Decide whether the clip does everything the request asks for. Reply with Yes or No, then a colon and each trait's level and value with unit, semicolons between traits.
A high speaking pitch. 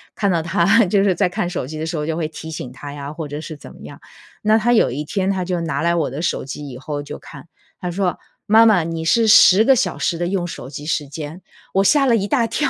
No: medium, 170 Hz